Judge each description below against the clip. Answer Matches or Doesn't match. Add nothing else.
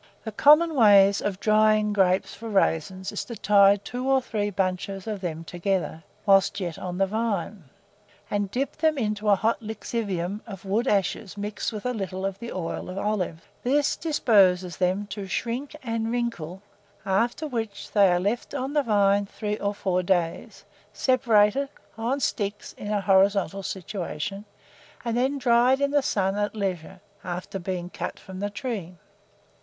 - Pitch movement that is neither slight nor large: Matches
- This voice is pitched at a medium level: Doesn't match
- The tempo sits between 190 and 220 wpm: Doesn't match